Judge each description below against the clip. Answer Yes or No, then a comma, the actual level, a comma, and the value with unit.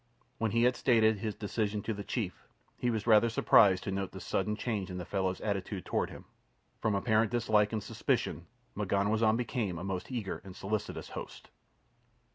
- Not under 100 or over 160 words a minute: No, average, 180 wpm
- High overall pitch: No, low, 105 Hz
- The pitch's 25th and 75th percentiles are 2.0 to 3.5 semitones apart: Yes, narrow, 2.4 semitones